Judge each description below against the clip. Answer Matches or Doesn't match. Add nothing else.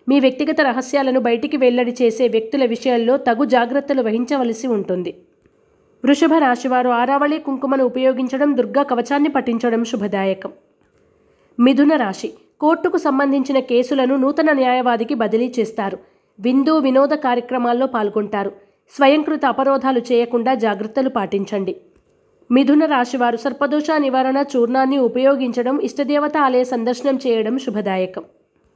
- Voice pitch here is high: Matches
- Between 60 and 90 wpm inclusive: Doesn't match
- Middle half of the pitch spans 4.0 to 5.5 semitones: Doesn't match